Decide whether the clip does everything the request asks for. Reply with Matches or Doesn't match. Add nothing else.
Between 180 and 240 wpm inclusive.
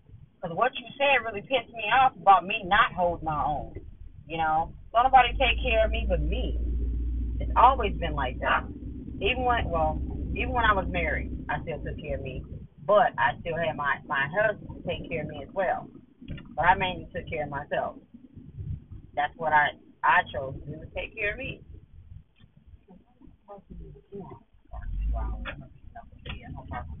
Doesn't match